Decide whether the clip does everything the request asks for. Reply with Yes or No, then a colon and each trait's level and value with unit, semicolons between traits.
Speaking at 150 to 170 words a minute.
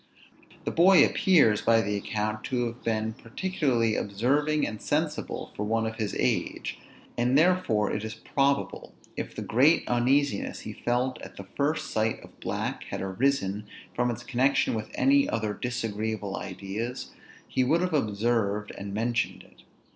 Yes: average, 155 wpm